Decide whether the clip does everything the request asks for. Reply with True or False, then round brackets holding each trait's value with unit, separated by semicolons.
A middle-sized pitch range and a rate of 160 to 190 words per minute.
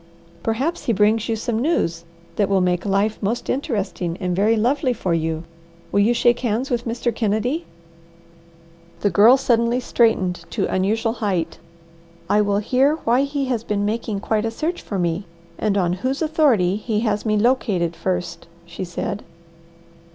True (3.9 semitones; 165 wpm)